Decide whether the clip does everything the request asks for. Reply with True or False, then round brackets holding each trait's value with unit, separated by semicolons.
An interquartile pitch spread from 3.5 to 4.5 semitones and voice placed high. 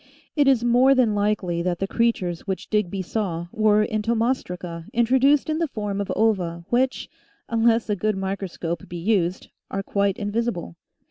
True (4.2 semitones; 210 Hz)